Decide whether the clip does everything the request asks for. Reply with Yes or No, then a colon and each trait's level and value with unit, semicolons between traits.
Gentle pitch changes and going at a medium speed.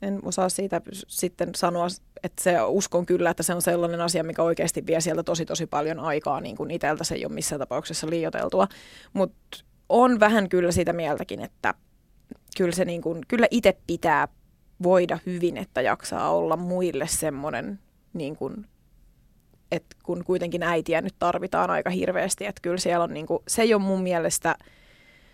No: narrow, 1.8 semitones; fast, 170 wpm